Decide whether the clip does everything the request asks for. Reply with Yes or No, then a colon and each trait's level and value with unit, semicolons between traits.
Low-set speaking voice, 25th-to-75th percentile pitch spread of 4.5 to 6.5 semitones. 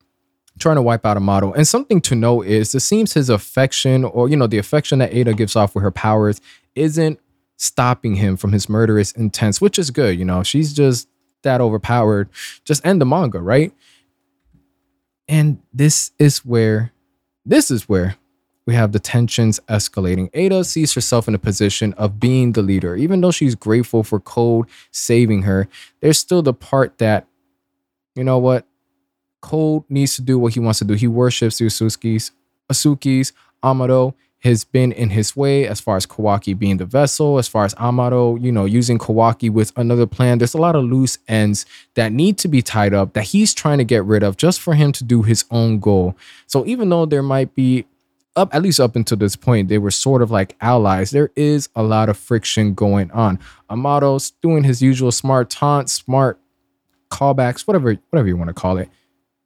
Yes: low, 115 Hz; average, 5.0 semitones